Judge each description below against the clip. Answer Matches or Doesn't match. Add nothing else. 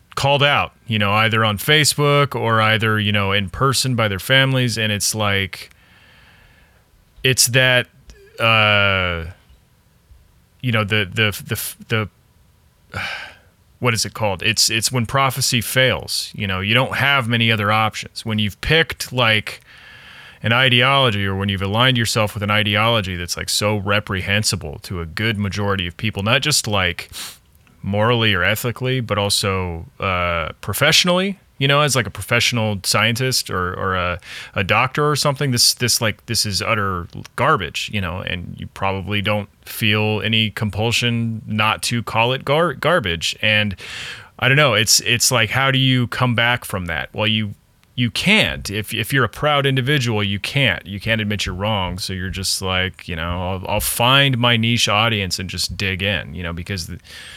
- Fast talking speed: Doesn't match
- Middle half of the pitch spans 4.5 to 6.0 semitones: Doesn't match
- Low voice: Matches